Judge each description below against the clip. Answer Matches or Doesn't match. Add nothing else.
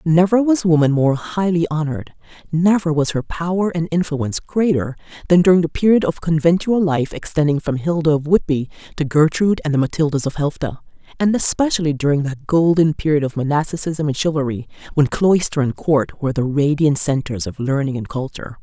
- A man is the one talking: Doesn't match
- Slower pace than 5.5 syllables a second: Doesn't match